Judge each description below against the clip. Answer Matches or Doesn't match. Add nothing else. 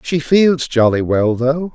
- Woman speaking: Doesn't match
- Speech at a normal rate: Matches